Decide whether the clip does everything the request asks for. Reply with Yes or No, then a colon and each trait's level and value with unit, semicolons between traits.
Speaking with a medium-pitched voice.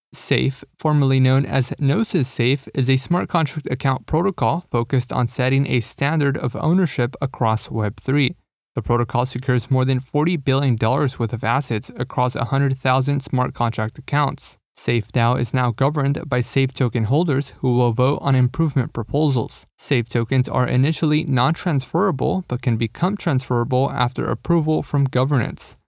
No: low, 130 Hz